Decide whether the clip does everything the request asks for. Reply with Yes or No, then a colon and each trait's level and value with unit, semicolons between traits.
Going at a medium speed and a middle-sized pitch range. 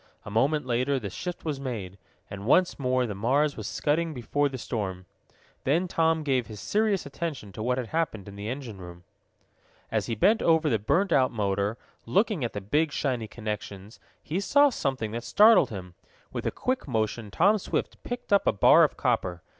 No: average, 195 wpm; wide, 7.3 semitones